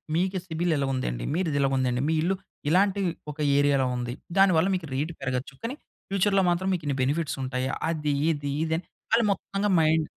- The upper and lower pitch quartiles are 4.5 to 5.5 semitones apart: Yes, average, 5.2 semitones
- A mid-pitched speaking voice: Yes, medium, 160 Hz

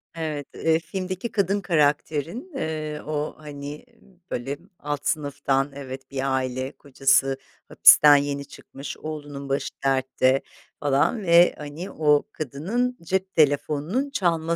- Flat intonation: No, average, 3.3 semitones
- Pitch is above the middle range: No, medium, 150 Hz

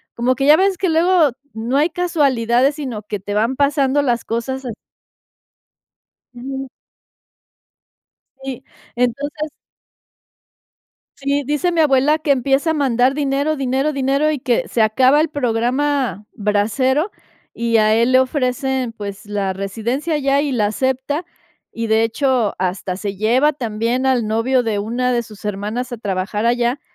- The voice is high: Yes, very high, 255 Hz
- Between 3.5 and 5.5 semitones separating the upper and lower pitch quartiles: Yes, average, 3.9 semitones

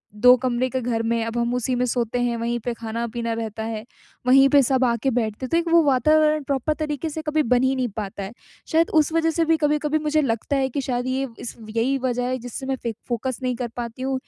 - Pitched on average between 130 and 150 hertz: No, very high, 255 Hz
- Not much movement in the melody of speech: No, average, 3.4 semitones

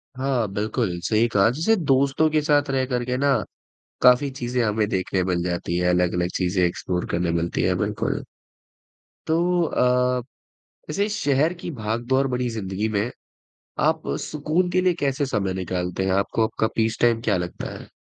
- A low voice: Yes, low, 120 Hz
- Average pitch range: No, wide, 6.9 semitones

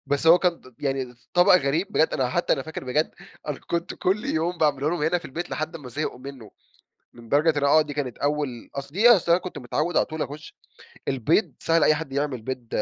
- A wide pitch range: No, average, 3.6 semitones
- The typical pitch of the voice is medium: Yes, medium, 150 Hz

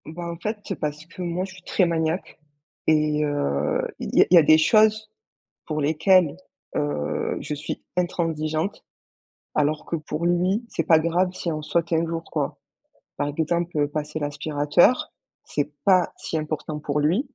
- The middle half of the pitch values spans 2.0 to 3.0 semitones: Yes, average, 2.7 semitones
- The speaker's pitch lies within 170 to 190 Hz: No, medium, 160 Hz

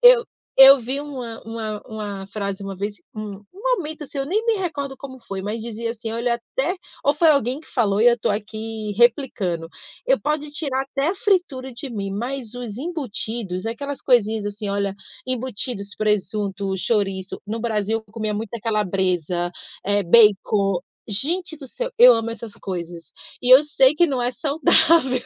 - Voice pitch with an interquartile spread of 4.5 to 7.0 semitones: Yes, average, 5.1 semitones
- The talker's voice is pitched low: No, high, 230 Hz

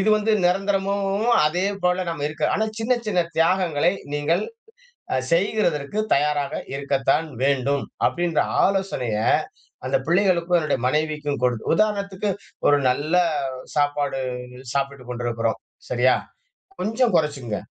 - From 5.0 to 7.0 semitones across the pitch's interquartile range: Yes, wide, 5.5 semitones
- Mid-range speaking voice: Yes, medium, 155 Hz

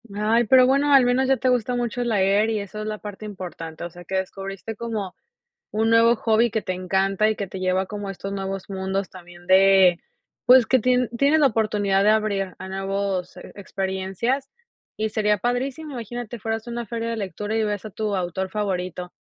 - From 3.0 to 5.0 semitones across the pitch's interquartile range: Yes, average, 3.3 semitones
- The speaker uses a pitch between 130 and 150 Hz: No, high, 210 Hz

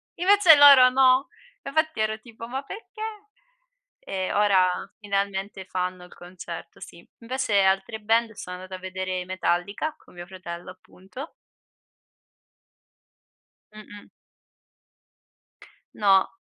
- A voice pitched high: Yes, high, 200 Hz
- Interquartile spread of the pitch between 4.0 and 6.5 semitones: Yes, average, 5.3 semitones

